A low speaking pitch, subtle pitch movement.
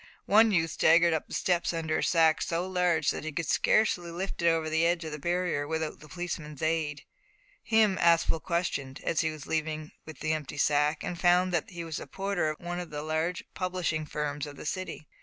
No: medium, 165 Hz; narrow, 2.2 semitones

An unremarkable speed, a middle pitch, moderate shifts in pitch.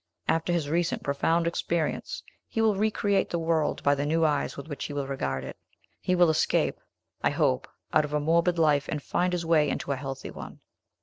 No: fast, 210 wpm; medium, 160 Hz; average, 3.1 semitones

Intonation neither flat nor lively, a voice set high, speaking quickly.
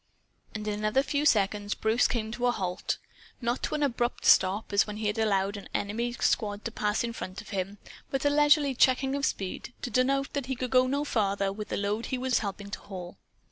Yes: average, 4.1 semitones; high, 220 Hz; fast, 225 wpm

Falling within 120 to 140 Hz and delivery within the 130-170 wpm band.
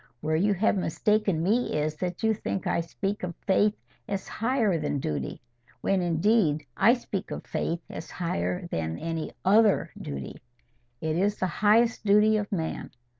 No: high, 190 Hz; average, 165 wpm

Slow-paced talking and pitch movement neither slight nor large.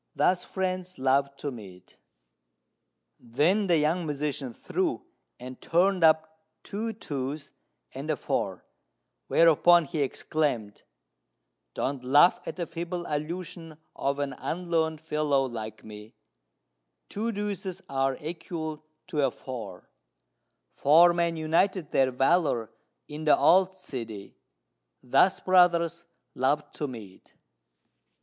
Yes: slow, 115 wpm; average, 4.5 semitones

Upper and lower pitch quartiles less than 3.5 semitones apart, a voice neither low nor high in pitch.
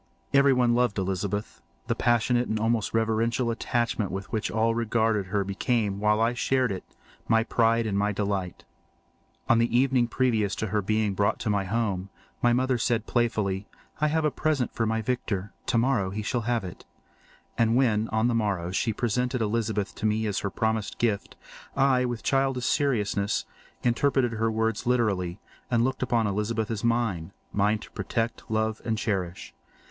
No: narrow, 2.6 semitones; low, 110 Hz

